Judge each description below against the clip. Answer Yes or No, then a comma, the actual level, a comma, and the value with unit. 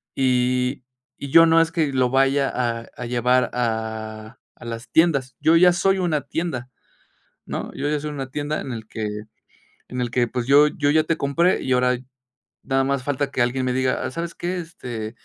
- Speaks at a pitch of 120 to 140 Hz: Yes, low, 135 Hz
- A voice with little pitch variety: No, average, 3.6 semitones